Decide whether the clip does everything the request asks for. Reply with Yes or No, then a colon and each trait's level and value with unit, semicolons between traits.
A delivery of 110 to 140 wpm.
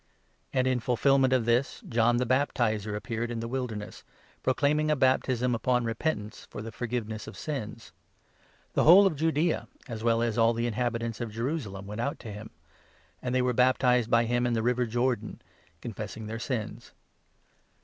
No: average, 180 wpm